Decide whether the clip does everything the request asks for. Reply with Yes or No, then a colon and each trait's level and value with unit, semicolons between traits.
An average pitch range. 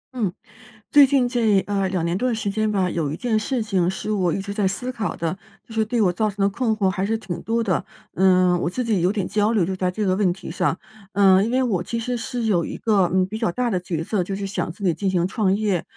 Yes: average, 3.3 semitones